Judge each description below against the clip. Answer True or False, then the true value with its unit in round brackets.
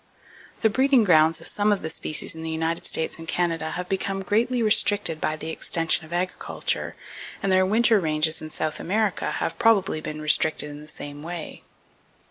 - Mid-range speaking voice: True (165 Hz)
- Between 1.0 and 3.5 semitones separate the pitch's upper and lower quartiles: False (4.3 semitones)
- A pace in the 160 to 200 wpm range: True (185 wpm)